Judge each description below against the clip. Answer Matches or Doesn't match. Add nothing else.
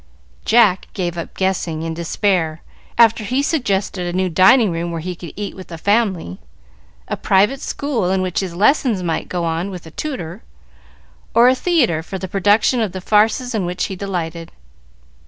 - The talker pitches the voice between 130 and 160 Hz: Doesn't match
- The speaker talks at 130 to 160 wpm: Doesn't match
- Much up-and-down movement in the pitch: Doesn't match